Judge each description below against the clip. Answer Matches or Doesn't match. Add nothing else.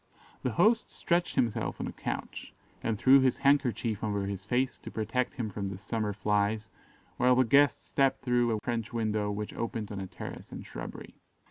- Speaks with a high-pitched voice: Doesn't match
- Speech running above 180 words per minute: Matches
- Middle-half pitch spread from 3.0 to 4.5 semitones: Matches